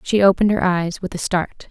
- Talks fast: Yes, fast, 245 wpm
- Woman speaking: Yes, female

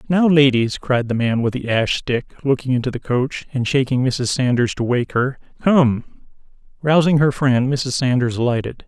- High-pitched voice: No, low, 130 Hz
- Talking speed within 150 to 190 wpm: Yes, average, 185 wpm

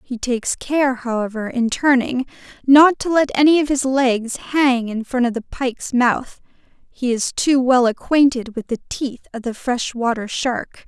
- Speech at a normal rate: Yes, average, 180 wpm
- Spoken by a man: No, female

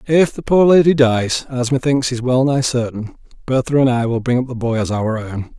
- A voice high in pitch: No, low, 125 Hz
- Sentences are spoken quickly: Yes, fast, 235 wpm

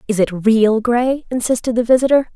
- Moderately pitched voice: No, high, 235 Hz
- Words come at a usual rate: Yes, average, 180 wpm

